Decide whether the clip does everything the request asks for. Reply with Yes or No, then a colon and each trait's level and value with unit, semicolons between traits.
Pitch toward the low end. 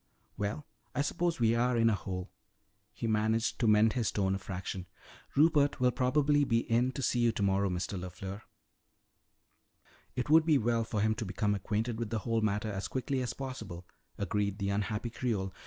Yes: low, 110 Hz